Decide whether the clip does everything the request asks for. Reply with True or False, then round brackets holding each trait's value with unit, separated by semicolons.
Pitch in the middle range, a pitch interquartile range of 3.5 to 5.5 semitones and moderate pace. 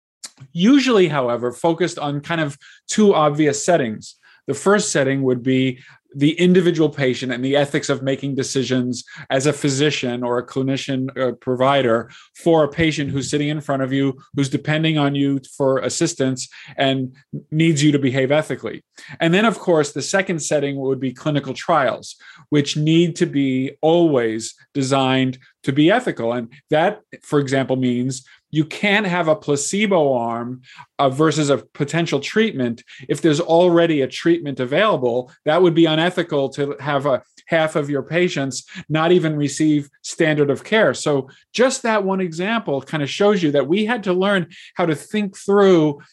True (145 Hz; 4.0 semitones; 170 wpm)